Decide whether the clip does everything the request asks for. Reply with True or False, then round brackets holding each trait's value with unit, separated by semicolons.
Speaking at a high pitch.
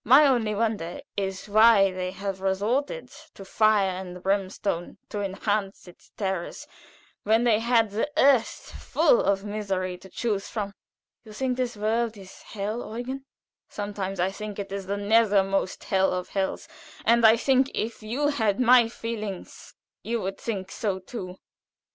True (210 Hz)